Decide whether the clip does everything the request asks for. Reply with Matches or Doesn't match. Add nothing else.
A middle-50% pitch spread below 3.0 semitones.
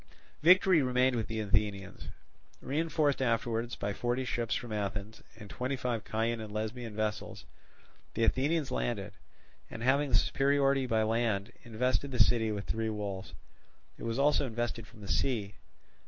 Doesn't match